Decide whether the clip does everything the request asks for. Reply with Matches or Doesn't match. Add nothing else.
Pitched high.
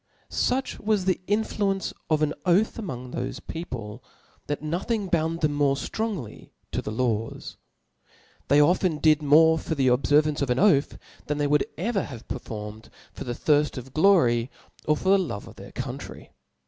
Doesn't match